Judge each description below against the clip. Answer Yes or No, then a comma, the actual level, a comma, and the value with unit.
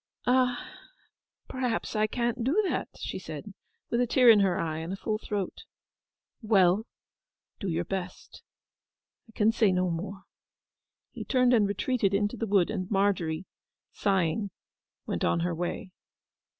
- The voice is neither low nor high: No, high, 205 Hz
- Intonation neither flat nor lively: Yes, average, 4.1 semitones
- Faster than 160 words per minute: No, average, 145 wpm